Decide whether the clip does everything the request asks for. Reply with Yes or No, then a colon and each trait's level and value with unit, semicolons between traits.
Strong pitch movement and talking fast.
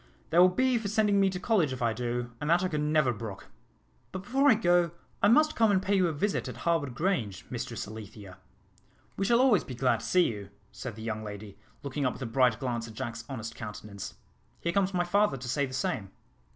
Yes: wide, 8.5 semitones; fast, 230 wpm